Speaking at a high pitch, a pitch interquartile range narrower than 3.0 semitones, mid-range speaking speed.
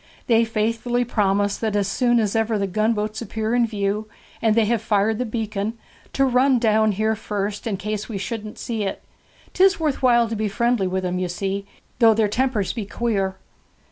Yes: high, 220 Hz; narrow, 2.4 semitones; average, 195 wpm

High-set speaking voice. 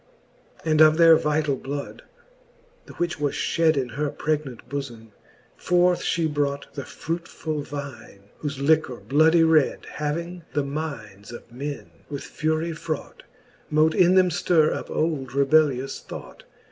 No: medium, 150 Hz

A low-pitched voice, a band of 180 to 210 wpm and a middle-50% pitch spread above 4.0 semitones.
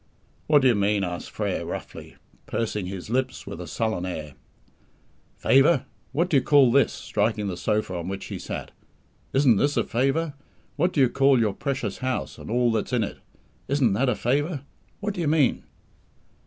Yes: low, 125 Hz; average, 185 wpm; average, 5.3 semitones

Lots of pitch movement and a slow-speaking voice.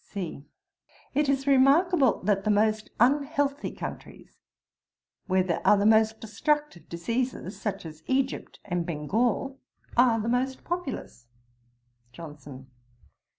Yes: wide, 6.7 semitones; slow, 115 wpm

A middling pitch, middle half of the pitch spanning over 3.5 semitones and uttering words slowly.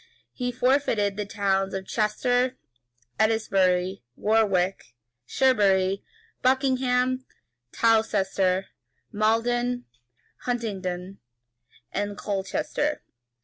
No: high, 215 Hz; average, 4.3 semitones; slow, 65 wpm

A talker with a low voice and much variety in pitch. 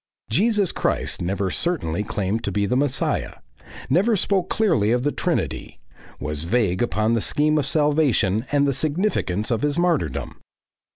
Yes: low, 130 Hz; wide, 7.5 semitones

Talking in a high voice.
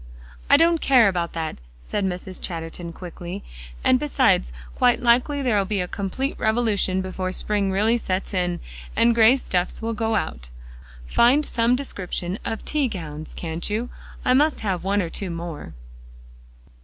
Yes: high, 200 Hz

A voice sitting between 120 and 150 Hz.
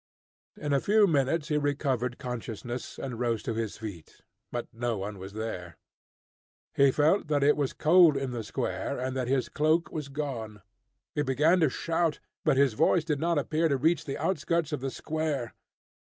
Yes: medium, 140 Hz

